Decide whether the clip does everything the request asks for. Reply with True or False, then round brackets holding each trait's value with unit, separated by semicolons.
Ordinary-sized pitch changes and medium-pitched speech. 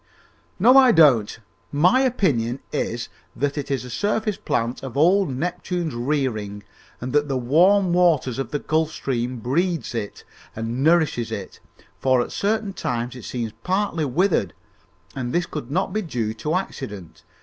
False (6.7 semitones; 145 Hz)